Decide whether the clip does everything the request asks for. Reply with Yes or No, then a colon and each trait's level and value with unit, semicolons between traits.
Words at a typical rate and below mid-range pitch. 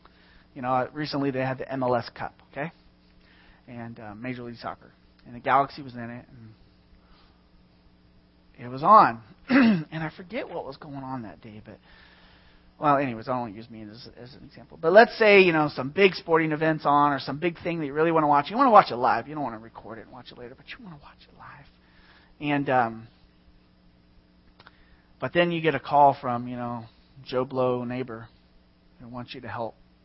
No: fast, 210 wpm; low, 120 Hz